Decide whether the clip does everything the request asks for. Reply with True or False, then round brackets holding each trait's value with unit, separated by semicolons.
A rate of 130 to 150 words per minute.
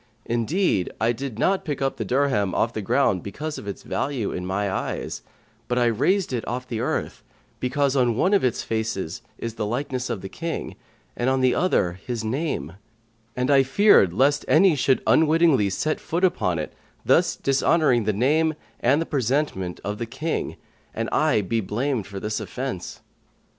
False (180 wpm)